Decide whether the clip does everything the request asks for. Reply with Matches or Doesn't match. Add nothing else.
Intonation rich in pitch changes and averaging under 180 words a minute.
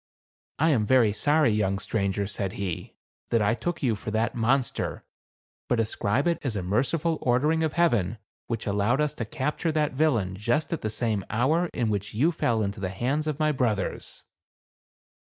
Doesn't match